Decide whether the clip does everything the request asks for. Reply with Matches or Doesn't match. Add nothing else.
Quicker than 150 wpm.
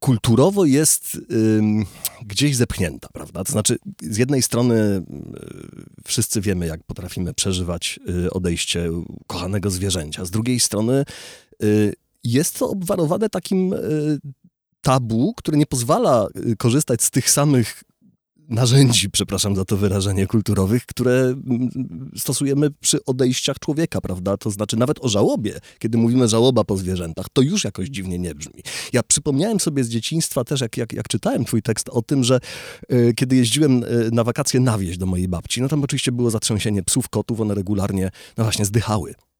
Matches